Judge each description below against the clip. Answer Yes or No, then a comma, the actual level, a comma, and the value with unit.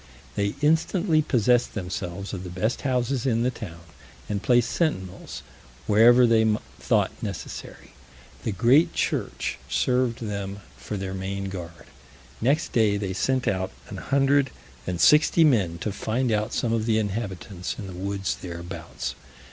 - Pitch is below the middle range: Yes, low, 110 Hz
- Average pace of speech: Yes, average, 150 wpm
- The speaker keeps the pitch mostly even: No, average, 4.6 semitones